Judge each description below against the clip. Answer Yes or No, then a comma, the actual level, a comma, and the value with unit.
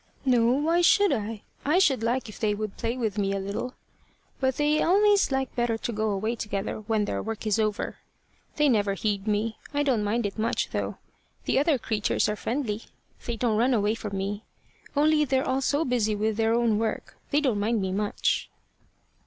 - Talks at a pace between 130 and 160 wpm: No, average, 200 wpm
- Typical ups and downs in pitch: Yes, average, 3.9 semitones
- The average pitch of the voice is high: Yes, high, 225 Hz